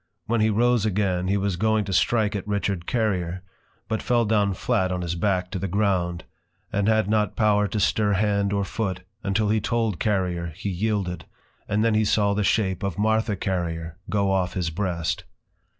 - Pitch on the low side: Yes, low, 100 Hz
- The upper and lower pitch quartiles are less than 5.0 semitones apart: Yes, average, 2.8 semitones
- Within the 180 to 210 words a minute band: Yes, average, 190 wpm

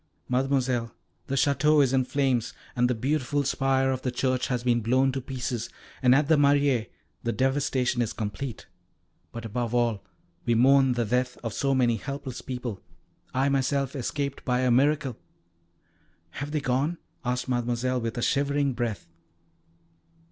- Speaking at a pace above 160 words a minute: No, average, 155 wpm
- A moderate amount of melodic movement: No, narrow, 2.2 semitones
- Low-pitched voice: Yes, low, 130 Hz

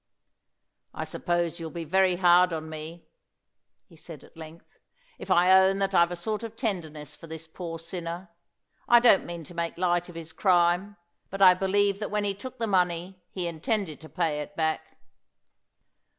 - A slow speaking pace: No, average, 180 wpm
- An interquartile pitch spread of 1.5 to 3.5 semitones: Yes, average, 2.8 semitones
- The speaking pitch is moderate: Yes, medium, 175 Hz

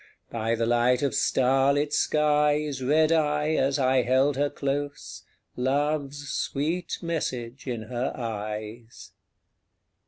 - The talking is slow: Yes, slow, 115 wpm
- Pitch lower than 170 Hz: Yes, low, 135 Hz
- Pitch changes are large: No, average, 3.5 semitones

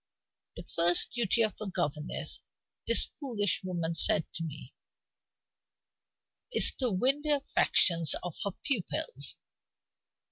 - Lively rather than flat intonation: Yes, wide, 6.7 semitones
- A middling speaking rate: No, slow, 115 wpm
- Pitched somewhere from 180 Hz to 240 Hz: Yes, medium, 185 Hz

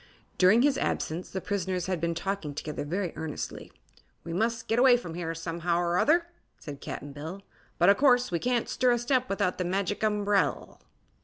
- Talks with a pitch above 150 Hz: Yes, high, 190 Hz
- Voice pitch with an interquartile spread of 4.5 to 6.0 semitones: Yes, average, 5.2 semitones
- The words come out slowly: No, average, 185 wpm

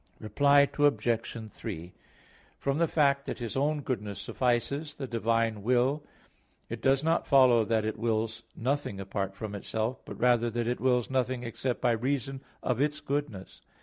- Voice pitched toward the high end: No, low, 125 Hz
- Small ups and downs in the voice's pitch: No, average, 3.7 semitones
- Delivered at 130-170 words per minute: Yes, average, 160 wpm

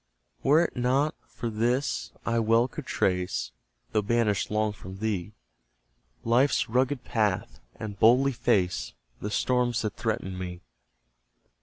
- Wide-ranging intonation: No, average, 3.5 semitones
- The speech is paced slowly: Yes, slow, 130 wpm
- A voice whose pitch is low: Yes, low, 110 Hz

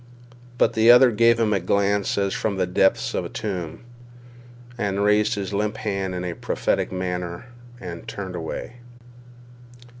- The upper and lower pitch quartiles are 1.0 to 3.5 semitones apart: Yes, average, 2.7 semitones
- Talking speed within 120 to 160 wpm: Yes, average, 155 wpm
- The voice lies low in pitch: Yes, low, 100 Hz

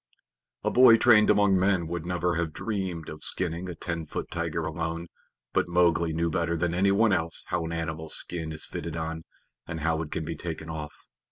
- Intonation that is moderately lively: No, narrow, 1.9 semitones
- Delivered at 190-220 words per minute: Yes, average, 195 wpm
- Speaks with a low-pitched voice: Yes, very low, 85 Hz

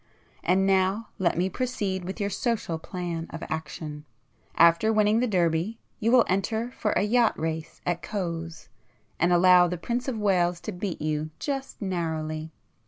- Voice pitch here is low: No, medium, 185 Hz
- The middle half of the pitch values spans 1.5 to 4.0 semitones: No, average, 4.4 semitones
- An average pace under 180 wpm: Yes, average, 165 wpm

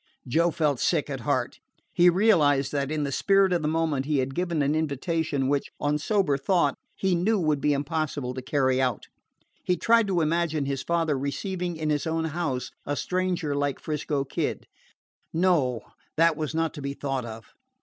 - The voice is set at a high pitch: No, medium, 155 Hz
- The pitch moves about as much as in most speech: Yes, average, 3.5 semitones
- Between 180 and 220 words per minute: Yes, average, 185 wpm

